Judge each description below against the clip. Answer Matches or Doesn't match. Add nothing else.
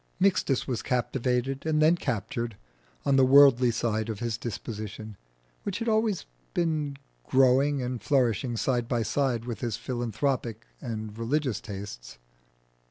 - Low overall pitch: Matches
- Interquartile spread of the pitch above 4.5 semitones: Doesn't match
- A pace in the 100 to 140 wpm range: Matches